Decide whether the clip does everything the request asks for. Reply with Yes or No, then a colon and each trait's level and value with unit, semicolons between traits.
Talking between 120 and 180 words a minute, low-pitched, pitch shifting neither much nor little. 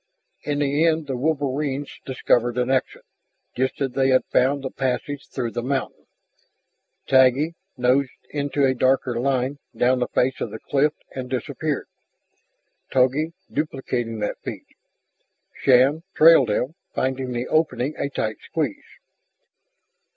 No: slow, 135 wpm; low, 130 Hz; narrow, 2.3 semitones